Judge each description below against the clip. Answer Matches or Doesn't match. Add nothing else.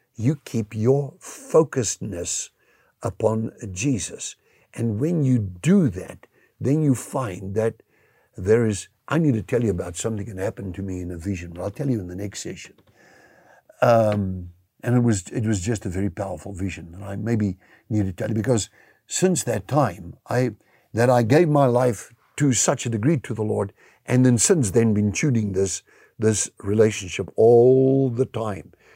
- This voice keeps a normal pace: Matches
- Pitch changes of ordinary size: Matches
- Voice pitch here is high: Doesn't match